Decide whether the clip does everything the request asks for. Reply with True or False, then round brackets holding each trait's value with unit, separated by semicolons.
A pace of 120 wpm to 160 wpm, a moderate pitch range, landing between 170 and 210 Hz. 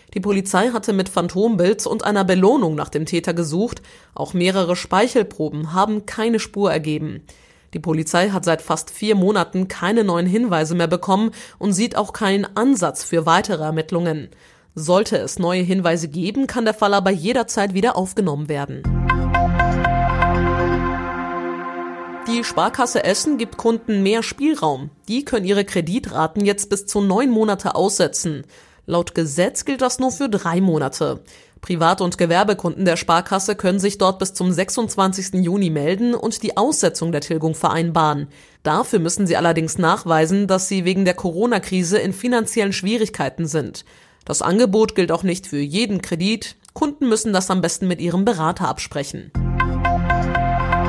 True (150 wpm; 4.2 semitones; 185 Hz)